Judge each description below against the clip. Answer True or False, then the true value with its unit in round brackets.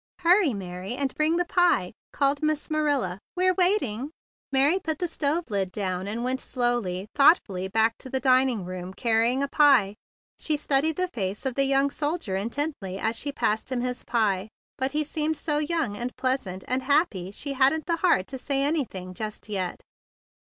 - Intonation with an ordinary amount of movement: False (6.5 semitones)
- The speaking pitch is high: True (265 Hz)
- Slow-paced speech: False (180 wpm)